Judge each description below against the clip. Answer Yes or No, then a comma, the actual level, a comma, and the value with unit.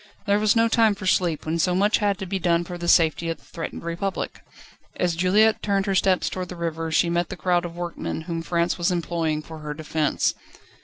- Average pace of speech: No, fast, 225 wpm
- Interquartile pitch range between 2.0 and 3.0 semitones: Yes, narrow, 2.5 semitones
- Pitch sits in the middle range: Yes, medium, 175 Hz